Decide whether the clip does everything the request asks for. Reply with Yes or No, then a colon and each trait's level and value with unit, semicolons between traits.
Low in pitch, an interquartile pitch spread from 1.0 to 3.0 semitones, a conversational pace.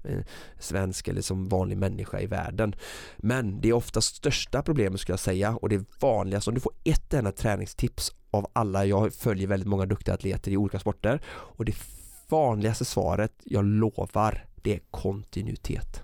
Yes: low, 100 Hz; narrow, 2.5 semitones; average, 170 wpm